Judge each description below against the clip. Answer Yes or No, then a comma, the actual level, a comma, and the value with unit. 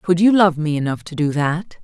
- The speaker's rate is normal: No, fast, 260 wpm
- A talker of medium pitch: Yes, medium, 165 Hz